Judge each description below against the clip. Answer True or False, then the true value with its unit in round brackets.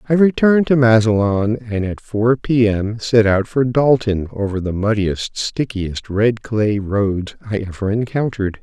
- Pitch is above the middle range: False (110 Hz)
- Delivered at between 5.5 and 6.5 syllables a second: False (4.3 syllables/s)